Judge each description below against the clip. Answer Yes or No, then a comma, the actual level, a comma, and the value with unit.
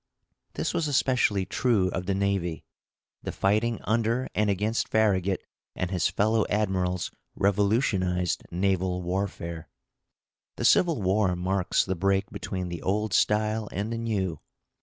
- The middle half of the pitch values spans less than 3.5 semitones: Yes, average, 2.8 semitones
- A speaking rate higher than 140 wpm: No, slow, 135 wpm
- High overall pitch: No, low, 100 Hz